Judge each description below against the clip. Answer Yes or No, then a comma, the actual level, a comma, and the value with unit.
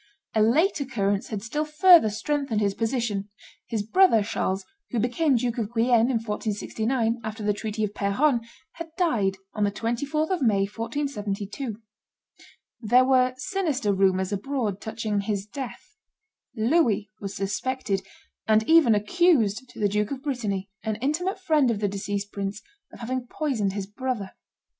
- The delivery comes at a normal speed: Yes, average, 150 wpm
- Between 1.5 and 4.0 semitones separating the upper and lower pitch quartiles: No, average, 4.6 semitones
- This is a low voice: No, high, 225 Hz